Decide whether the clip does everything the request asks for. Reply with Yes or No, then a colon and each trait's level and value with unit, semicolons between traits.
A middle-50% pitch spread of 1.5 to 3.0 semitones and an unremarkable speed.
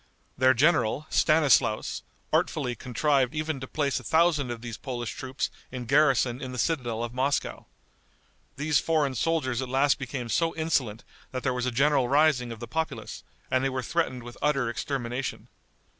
No: average, 3.4 semitones; average, 170 wpm